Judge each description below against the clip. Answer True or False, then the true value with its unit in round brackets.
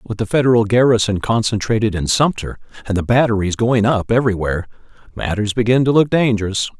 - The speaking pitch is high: False (110 Hz)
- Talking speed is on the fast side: False (160 wpm)